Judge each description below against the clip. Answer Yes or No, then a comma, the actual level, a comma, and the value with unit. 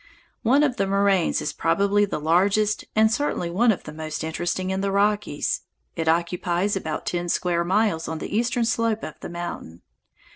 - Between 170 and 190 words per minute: Yes, average, 180 wpm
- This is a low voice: No, high, 190 Hz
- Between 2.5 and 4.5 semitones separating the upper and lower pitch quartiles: Yes, average, 3.9 semitones